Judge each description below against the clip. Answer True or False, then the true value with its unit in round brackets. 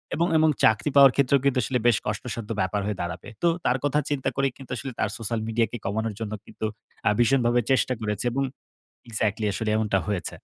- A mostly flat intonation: False (4.0 semitones)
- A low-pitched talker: True (115 Hz)